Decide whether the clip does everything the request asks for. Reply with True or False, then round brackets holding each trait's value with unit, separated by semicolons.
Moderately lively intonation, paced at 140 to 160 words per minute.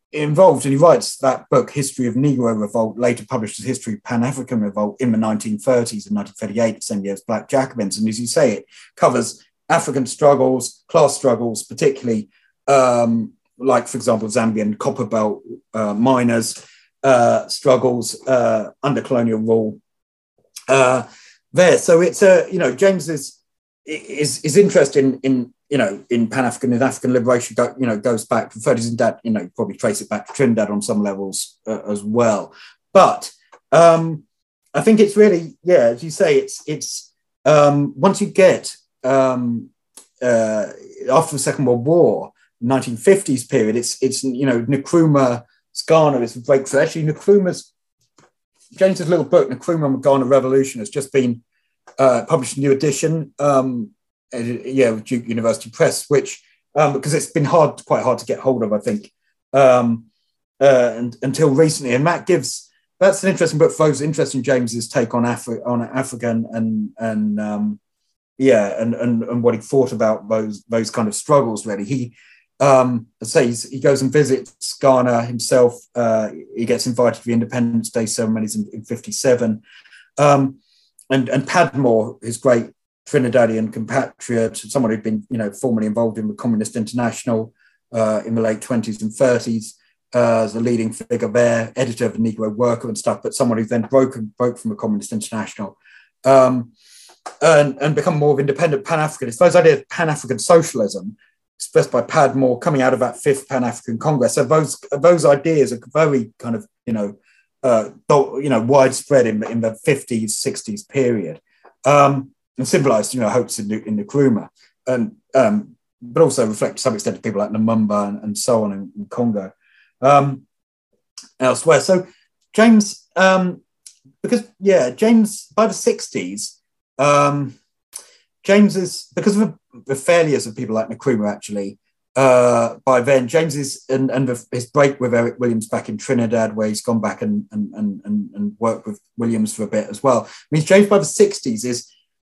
False (4.5 semitones; 175 wpm)